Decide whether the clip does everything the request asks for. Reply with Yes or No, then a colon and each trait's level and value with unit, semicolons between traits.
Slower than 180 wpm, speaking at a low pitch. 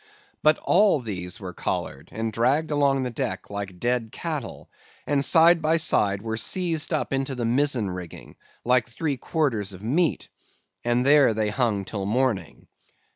Yes: average, 160 wpm; low, 125 Hz